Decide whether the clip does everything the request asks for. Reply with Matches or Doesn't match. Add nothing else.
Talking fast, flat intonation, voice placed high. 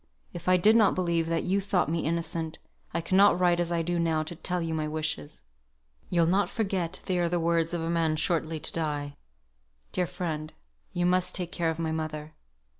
Doesn't match